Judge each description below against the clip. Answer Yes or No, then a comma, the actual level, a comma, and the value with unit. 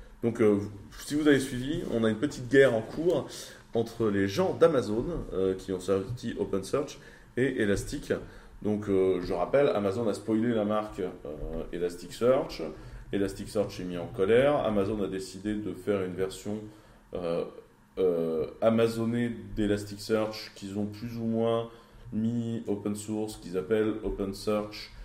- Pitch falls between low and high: No, low, 105 Hz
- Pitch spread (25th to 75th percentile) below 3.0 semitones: Yes, narrow, 2.6 semitones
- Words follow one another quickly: No, average, 150 wpm